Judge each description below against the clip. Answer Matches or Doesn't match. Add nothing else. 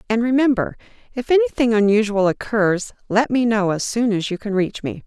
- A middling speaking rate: Matches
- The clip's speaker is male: Doesn't match